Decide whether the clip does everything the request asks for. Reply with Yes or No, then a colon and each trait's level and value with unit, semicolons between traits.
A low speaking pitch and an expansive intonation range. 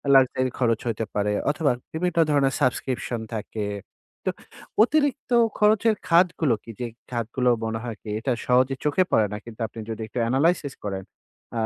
Yes: low, 130 Hz; wide, 6.0 semitones